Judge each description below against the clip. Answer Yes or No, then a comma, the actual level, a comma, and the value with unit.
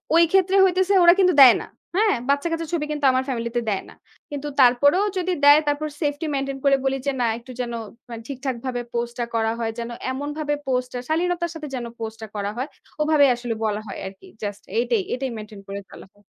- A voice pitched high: Yes, very high, 270 Hz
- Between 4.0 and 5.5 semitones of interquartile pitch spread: Yes, average, 4.6 semitones